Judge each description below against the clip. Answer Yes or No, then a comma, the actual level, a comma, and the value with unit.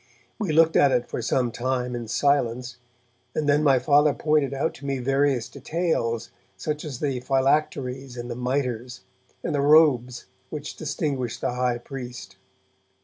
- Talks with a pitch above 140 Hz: No, low, 135 Hz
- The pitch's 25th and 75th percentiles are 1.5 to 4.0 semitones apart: Yes, average, 2.9 semitones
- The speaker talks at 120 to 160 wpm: Yes, average, 155 wpm